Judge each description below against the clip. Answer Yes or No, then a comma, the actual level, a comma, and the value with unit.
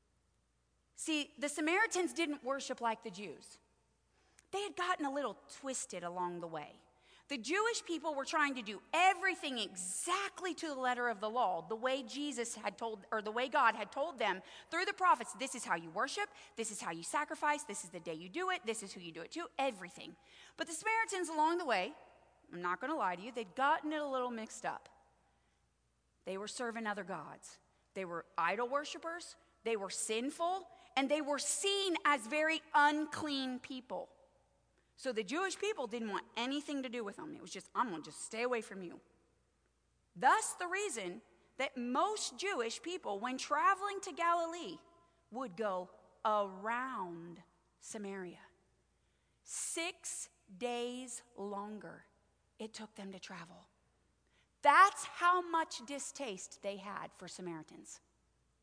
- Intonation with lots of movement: Yes, wide, 7.6 semitones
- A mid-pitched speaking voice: No, very high, 265 Hz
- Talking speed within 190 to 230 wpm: No, average, 165 wpm